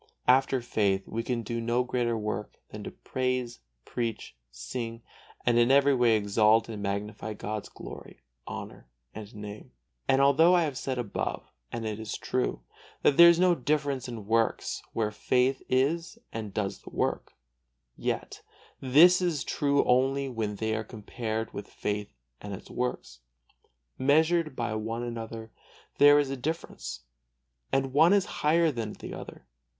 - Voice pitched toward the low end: Yes, low, 120 Hz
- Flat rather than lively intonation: No, average, 4.2 semitones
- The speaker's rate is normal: Yes, average, 155 wpm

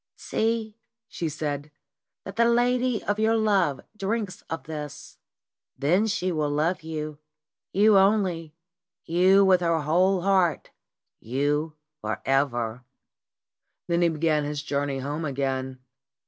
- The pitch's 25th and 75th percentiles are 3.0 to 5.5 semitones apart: Yes, average, 5.2 semitones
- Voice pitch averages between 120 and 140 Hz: No, medium, 165 Hz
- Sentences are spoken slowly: Yes, slow, 125 wpm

